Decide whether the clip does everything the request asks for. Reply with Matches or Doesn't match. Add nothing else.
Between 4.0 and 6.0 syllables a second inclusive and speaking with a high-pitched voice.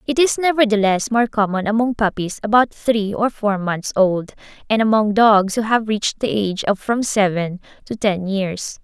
Matches